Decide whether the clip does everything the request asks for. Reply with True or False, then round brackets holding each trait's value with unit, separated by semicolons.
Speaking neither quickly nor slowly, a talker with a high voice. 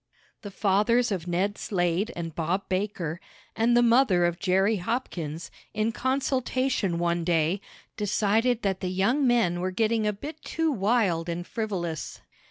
True (150 wpm; 200 Hz)